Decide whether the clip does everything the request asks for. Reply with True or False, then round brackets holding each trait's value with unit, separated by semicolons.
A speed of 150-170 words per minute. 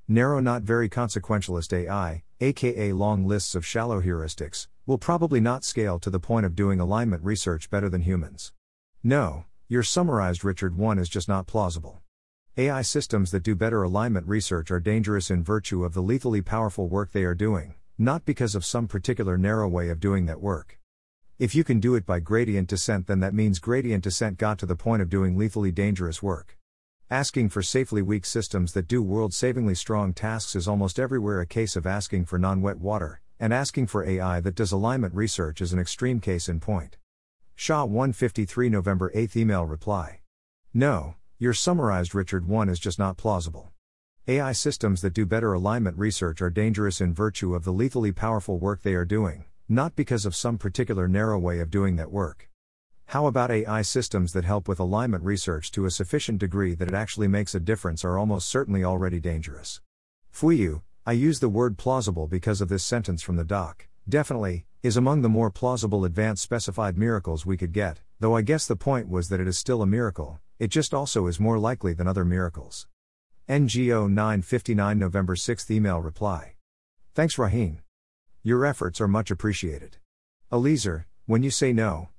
False (185 wpm)